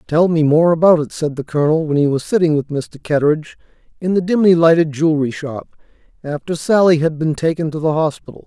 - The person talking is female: No, male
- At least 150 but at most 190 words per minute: No, fast, 205 wpm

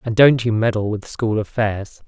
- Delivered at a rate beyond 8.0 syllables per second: No, 4.7 syllables/s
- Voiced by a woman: No, male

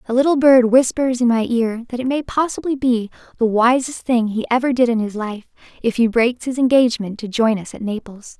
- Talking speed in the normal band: No, fast, 220 wpm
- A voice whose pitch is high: Yes, high, 240 Hz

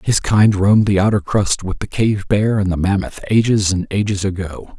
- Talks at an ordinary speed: No, fast, 215 wpm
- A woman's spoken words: No, male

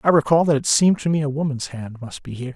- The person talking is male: Yes, male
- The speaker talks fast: Yes, fast, 305 wpm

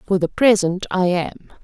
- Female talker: Yes, female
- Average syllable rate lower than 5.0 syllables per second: Yes, 4.4 syllables/s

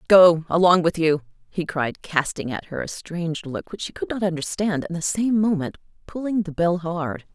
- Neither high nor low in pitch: Yes, medium, 170 Hz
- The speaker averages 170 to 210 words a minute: Yes, fast, 205 wpm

